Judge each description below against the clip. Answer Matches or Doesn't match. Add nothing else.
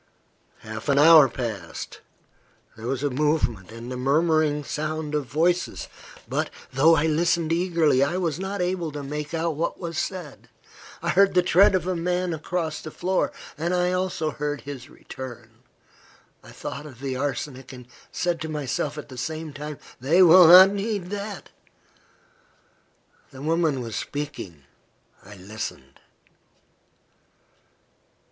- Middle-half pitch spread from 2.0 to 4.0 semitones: Doesn't match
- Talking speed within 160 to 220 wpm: Doesn't match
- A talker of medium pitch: Matches